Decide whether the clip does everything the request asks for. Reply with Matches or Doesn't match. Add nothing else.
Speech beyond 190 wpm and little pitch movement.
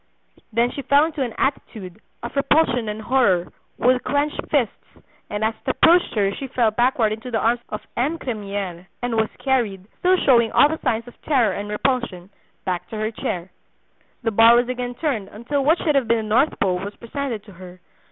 Doesn't match